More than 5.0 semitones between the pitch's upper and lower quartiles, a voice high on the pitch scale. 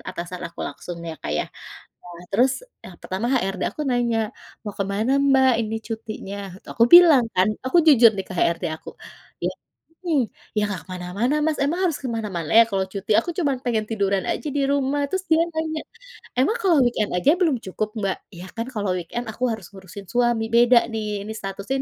Yes: wide, 5.5 semitones; high, 225 Hz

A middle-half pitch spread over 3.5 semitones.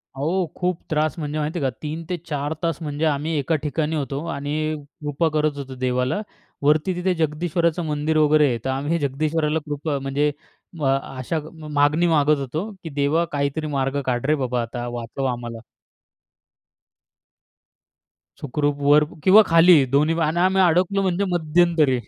No: average, 2.7 semitones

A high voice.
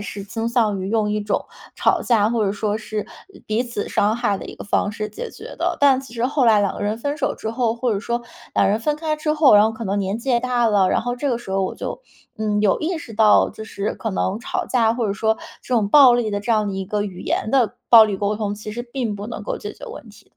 Yes: high, 220 Hz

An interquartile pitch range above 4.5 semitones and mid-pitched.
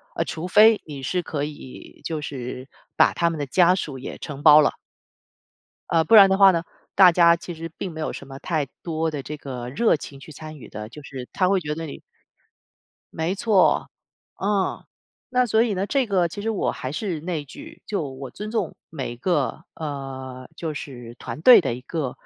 Yes: average, 5.2 semitones; medium, 160 Hz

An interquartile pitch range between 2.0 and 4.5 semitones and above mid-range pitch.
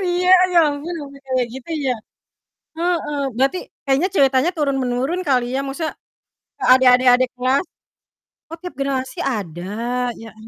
Yes: average, 3.0 semitones; very high, 270 Hz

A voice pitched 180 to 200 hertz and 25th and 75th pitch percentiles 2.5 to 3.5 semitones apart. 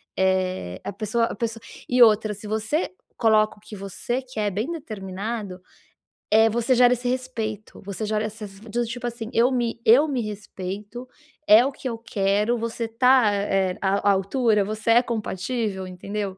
No: high, 220 Hz; average, 2.9 semitones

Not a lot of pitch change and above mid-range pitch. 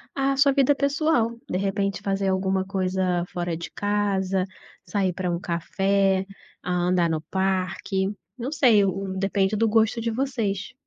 No: average, 3.1 semitones; high, 195 Hz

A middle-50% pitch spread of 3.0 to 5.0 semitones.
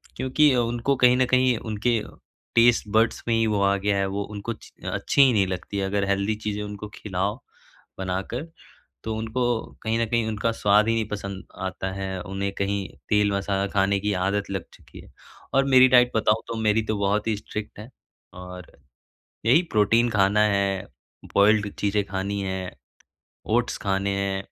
No: narrow, 2.4 semitones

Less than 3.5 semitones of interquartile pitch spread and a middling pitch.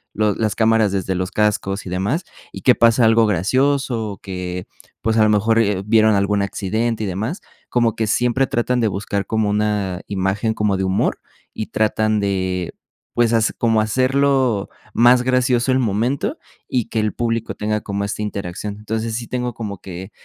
No: average, 2.8 semitones; low, 110 Hz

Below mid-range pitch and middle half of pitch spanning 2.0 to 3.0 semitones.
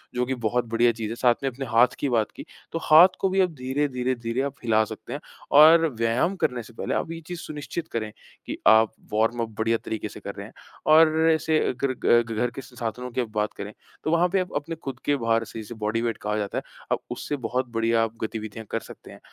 No: low, 120 Hz; average, 4.4 semitones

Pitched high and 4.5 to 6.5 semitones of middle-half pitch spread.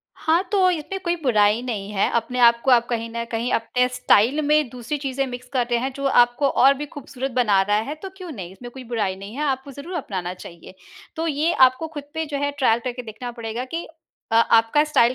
No: very high, 250 Hz; average, 4.0 semitones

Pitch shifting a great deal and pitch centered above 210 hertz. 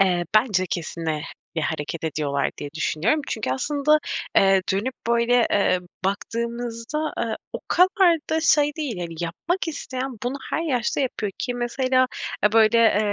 Yes: wide, 6.1 semitones; high, 230 Hz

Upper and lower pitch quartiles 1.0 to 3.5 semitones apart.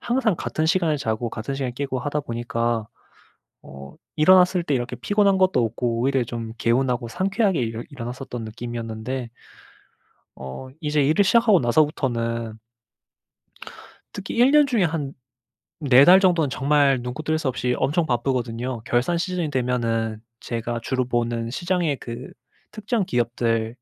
No: wide, 5.5 semitones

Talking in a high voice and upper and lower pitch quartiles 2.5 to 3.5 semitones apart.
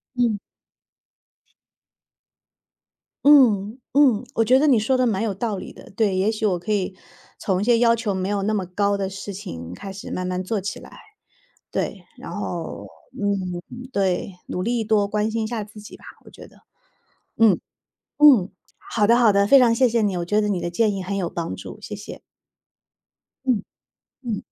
Yes: high, 210 Hz; average, 3.1 semitones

